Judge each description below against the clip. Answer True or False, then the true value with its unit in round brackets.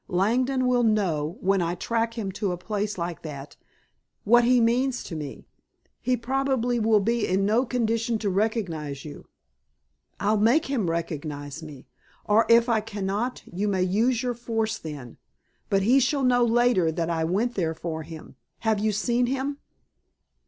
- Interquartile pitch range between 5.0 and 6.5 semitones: True (5.6 semitones)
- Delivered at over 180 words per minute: False (165 wpm)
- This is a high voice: True (215 Hz)